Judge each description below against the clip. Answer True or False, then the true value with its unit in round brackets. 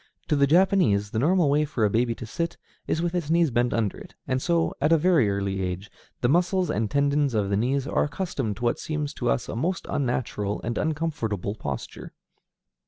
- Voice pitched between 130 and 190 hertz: True (135 Hz)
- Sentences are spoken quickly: True (210 wpm)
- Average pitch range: False (6.6 semitones)